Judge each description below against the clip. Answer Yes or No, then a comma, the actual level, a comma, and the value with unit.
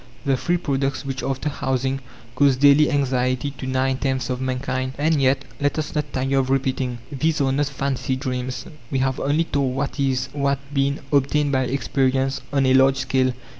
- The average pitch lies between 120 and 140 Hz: Yes, low, 135 Hz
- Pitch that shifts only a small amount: Yes, narrow, 1.4 semitones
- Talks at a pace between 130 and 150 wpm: No, average, 185 wpm